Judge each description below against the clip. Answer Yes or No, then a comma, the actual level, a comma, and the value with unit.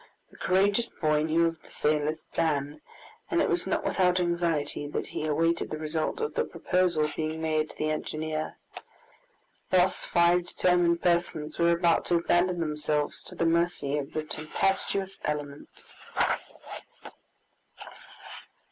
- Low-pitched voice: No, medium, 165 Hz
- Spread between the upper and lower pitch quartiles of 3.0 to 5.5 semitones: No, narrow, 2.4 semitones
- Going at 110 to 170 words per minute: Yes, average, 140 wpm